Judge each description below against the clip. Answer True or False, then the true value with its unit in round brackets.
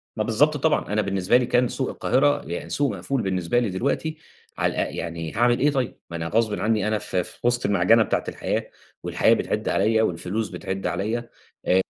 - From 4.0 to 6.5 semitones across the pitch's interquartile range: True (4.6 semitones)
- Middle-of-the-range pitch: False (110 Hz)